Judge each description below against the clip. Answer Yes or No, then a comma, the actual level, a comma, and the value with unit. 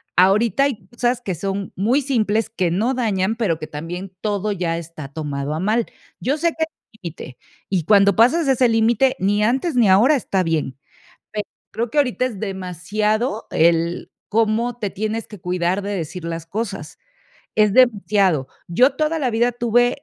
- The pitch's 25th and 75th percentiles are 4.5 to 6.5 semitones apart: Yes, average, 4.9 semitones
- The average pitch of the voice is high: Yes, high, 210 Hz